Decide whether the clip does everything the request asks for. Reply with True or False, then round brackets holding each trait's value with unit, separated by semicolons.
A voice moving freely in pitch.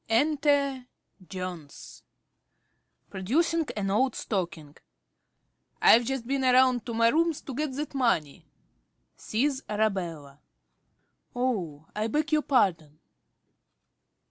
True (6.8 semitones)